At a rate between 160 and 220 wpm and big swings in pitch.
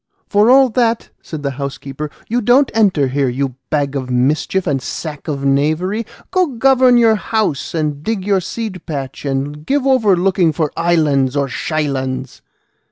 Yes: average, 165 wpm; wide, 8.0 semitones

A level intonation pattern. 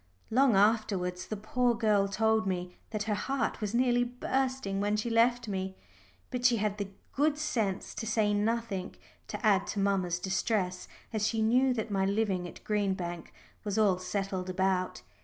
No: average, 3.2 semitones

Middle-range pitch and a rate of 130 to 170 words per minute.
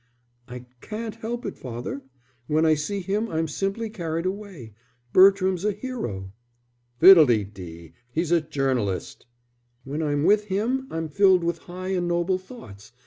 Yes: medium, 175 Hz; average, 140 wpm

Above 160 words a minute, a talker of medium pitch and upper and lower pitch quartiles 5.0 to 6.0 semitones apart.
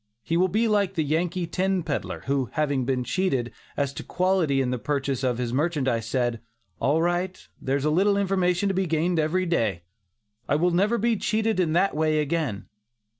Yes: average, 190 wpm; medium, 160 Hz; wide, 5.4 semitones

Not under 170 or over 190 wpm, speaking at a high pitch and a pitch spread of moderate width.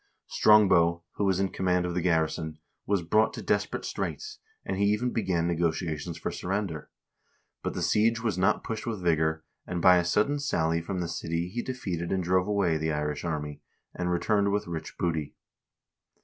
No: average, 180 wpm; very low, 90 Hz; average, 3.5 semitones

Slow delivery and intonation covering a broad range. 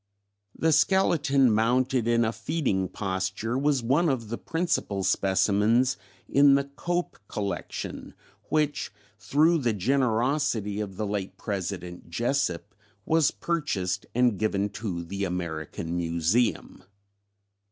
Yes: slow, 115 wpm; wide, 6.2 semitones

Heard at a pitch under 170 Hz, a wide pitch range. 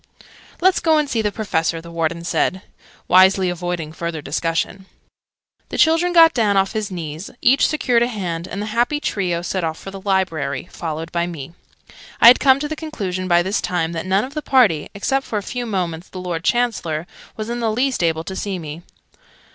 No: high, 190 Hz; wide, 5.9 semitones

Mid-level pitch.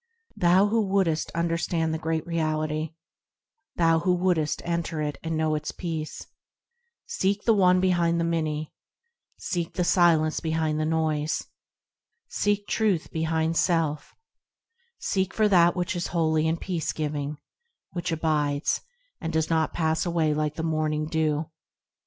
Yes: medium, 160 Hz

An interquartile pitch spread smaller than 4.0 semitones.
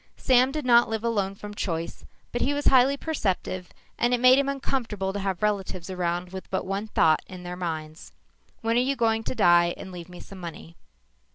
No: wide, 5.4 semitones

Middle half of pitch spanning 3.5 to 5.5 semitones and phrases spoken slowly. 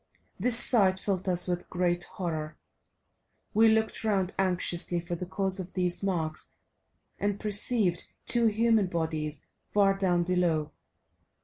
No: average, 2.8 semitones; slow, 130 wpm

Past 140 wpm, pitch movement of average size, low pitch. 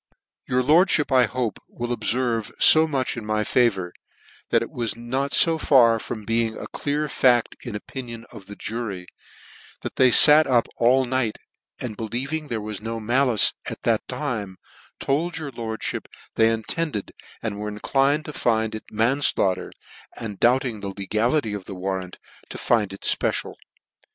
Yes: average, 165 wpm; average, 3.5 semitones; low, 115 Hz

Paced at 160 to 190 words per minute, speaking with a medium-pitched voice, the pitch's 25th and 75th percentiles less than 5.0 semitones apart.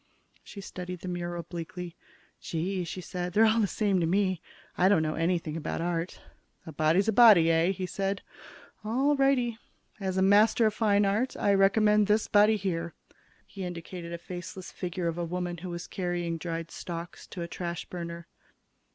Yes: average, 180 wpm; medium, 180 Hz; average, 3.1 semitones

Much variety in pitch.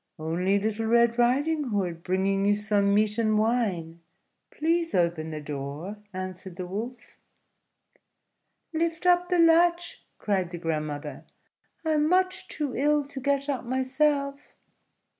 Yes: wide, 8.0 semitones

